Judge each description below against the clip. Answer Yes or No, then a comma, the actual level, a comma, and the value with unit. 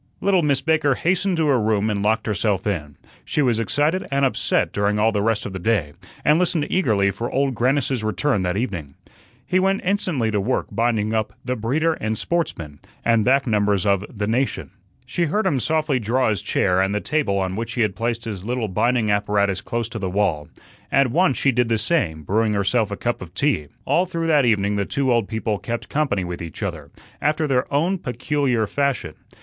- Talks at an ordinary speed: No, fast, 210 wpm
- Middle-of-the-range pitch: No, low, 115 Hz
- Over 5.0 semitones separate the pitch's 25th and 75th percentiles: Yes, wide, 5.4 semitones